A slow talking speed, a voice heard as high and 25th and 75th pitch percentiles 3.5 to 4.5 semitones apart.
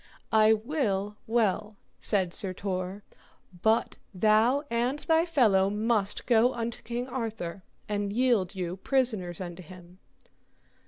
Yes: slow, 120 wpm; high, 215 Hz; average, 3.8 semitones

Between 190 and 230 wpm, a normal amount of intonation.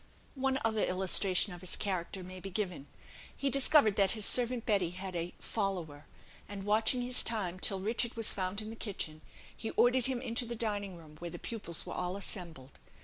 Yes: average, 195 wpm; average, 4.0 semitones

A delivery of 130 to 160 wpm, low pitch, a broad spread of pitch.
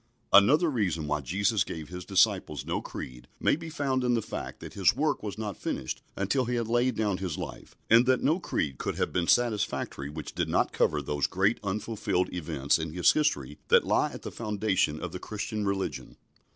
No: fast, 205 wpm; low, 100 Hz; wide, 5.9 semitones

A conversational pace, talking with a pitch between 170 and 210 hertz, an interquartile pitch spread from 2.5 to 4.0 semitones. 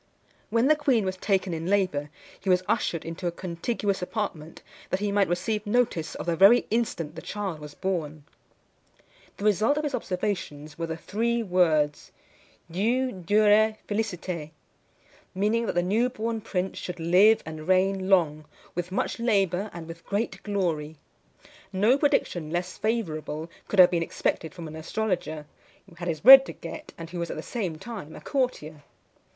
No: average, 170 wpm; medium, 185 Hz; average, 4.6 semitones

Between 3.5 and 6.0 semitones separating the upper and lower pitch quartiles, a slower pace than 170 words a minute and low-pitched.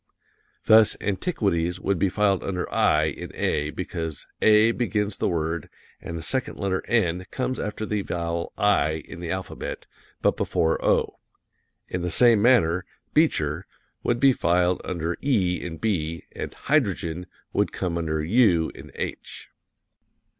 Yes: average, 4.2 semitones; average, 145 wpm; very low, 90 Hz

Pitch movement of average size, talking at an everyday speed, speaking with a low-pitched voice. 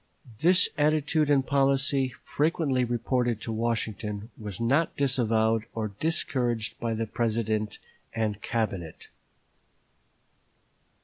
No: average, 3.9 semitones; slow, 100 wpm; low, 120 Hz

